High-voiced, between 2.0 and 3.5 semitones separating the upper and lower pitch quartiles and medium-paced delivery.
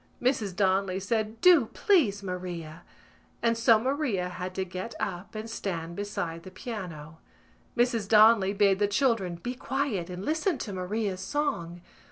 No: high, 200 Hz; average, 4.2 semitones; average, 150 wpm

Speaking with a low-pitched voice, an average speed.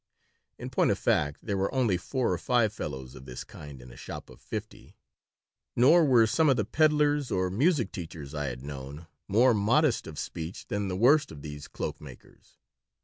Yes: low, 100 Hz; average, 195 wpm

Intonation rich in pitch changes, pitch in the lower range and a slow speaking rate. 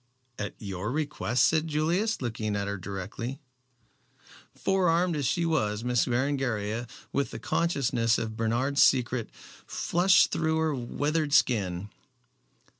Yes: wide, 6.2 semitones; low, 130 Hz; slow, 120 wpm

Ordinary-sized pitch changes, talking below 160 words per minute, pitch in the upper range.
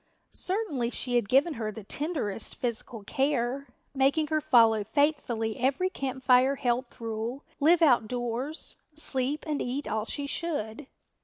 Yes: average, 3.9 semitones; average, 140 wpm; very high, 260 Hz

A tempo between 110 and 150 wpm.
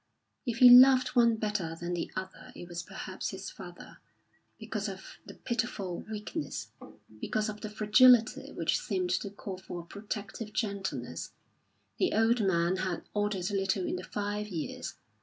No: average, 160 wpm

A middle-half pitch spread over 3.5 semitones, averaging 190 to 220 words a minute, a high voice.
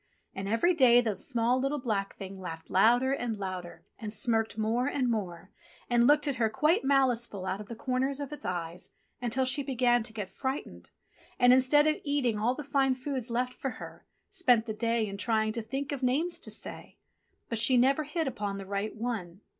Yes: average, 3.9 semitones; average, 200 wpm; high, 240 Hz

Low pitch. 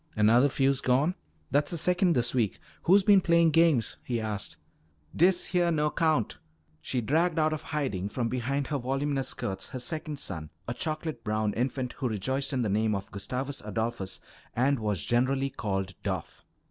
Yes: low, 130 Hz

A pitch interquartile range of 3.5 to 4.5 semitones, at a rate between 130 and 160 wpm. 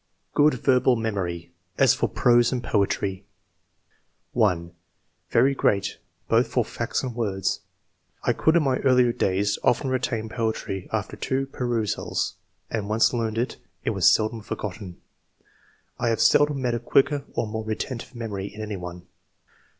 Yes: average, 3.8 semitones; average, 150 wpm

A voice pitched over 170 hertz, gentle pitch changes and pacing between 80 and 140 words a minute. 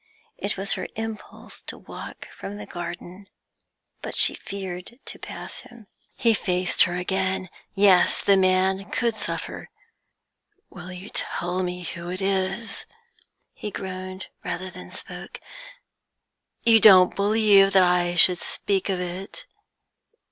Yes: high, 190 Hz; narrow, 1.8 semitones; slow, 135 wpm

